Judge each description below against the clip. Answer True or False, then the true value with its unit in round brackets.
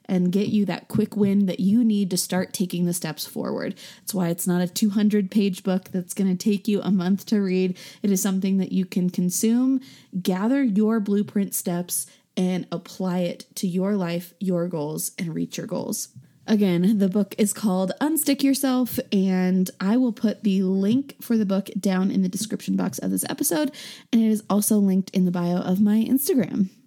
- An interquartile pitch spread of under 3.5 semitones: True (2.8 semitones)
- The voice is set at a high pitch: True (195 Hz)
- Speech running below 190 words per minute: False (200 wpm)